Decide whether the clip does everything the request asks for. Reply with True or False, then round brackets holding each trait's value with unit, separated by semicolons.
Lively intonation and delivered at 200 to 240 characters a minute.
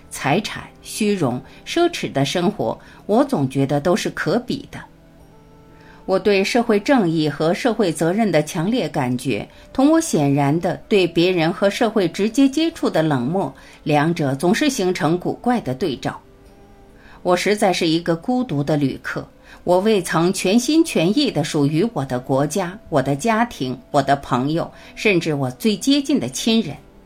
True (6.9 semitones; 235 characters per minute)